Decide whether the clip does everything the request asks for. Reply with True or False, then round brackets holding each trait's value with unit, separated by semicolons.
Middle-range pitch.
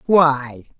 True (145 Hz)